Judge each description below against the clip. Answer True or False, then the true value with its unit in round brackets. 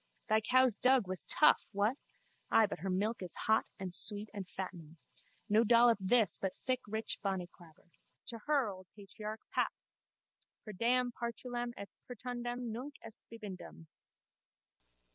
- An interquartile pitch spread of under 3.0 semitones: False (4.0 semitones)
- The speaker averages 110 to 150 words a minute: True (145 wpm)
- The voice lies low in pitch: False (220 Hz)